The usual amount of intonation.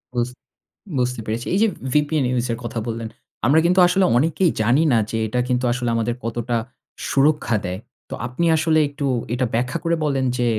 Yes: average, 4.1 semitones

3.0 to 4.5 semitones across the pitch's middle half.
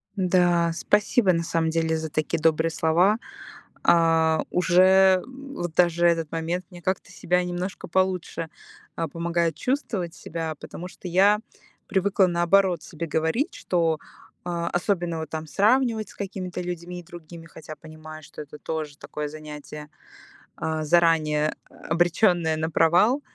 No: narrow, 2.4 semitones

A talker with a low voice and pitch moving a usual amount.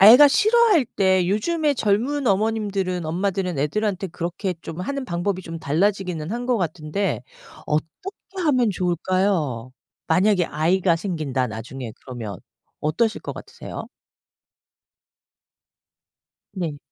No: medium, 185 Hz; average, 5.0 semitones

